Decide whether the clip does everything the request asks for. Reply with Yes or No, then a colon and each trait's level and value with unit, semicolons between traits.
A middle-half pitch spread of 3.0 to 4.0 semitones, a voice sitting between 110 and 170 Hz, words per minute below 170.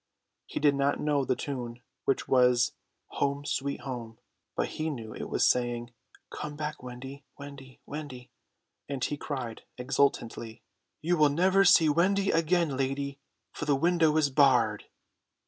Yes: average, 3.3 semitones; medium, 140 Hz; average, 145 wpm